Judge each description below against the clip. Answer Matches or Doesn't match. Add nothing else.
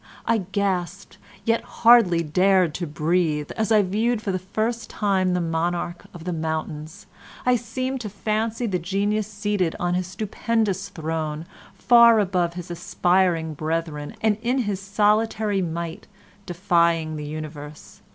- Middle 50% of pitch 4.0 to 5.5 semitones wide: Matches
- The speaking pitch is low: Doesn't match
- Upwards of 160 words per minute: Doesn't match